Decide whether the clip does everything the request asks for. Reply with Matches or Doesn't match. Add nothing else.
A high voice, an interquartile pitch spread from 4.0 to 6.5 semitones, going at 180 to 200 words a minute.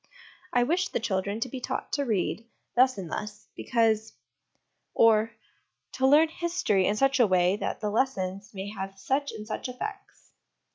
Matches